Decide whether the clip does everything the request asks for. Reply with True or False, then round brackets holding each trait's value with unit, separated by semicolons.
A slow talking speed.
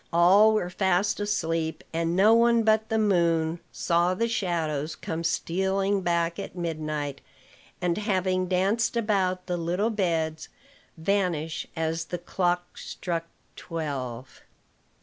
True (125 wpm)